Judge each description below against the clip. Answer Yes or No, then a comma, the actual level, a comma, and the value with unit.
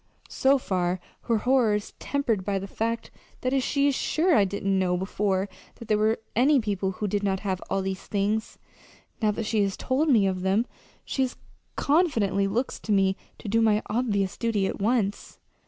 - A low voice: No, high, 210 Hz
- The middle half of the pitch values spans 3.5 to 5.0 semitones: Yes, average, 3.8 semitones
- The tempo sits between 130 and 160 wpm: No, average, 190 wpm